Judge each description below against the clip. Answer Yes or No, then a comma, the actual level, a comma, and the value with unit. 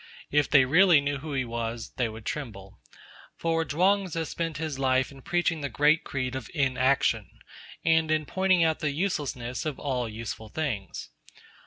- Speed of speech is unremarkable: Yes, average, 170 wpm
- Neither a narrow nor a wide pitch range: Yes, average, 4.1 semitones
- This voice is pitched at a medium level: Yes, medium, 145 Hz